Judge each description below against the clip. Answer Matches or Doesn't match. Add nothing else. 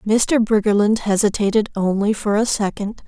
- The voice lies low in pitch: Doesn't match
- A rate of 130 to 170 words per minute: Matches